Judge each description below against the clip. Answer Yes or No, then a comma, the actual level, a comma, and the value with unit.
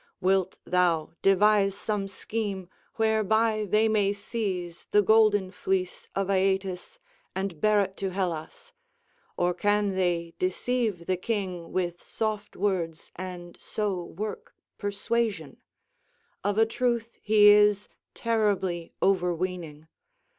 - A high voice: Yes, high, 195 Hz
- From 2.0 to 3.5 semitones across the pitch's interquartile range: Yes, average, 2.8 semitones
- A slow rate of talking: Yes, slow, 115 wpm